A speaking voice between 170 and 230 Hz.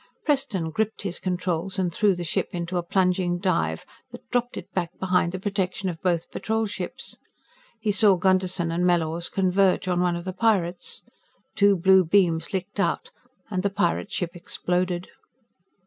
Yes: medium, 185 Hz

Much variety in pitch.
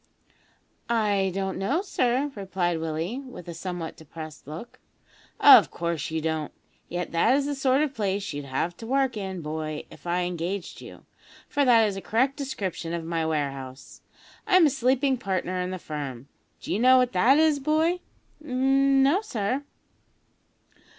Yes: wide, 8.1 semitones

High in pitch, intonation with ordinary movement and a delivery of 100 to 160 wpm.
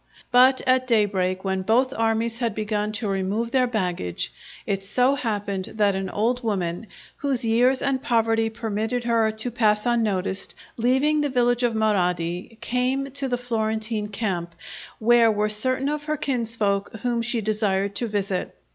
Yes: high, 225 Hz; average, 3.4 semitones; average, 155 wpm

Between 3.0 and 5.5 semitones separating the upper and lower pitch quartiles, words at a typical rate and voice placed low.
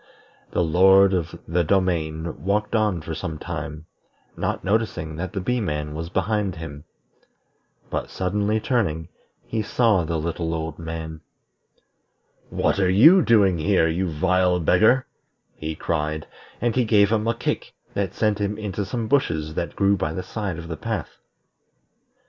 Yes: average, 4.6 semitones; average, 155 wpm; very low, 90 Hz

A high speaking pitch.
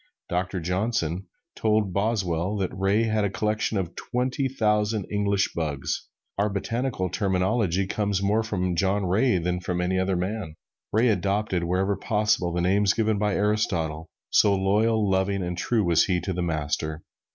No: low, 100 Hz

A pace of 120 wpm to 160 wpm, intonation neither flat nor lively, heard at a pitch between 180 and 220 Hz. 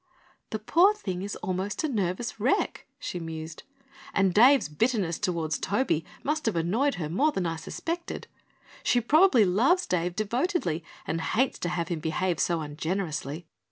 No: average, 155 wpm; wide, 7.1 semitones; high, 190 Hz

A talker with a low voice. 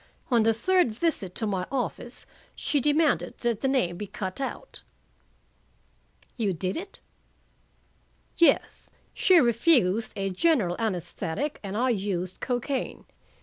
No: high, 230 Hz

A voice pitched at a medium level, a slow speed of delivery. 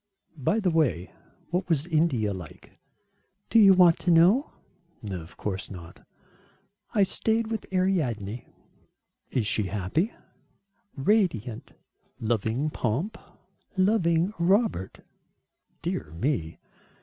Yes: medium, 155 Hz; slow, 100 wpm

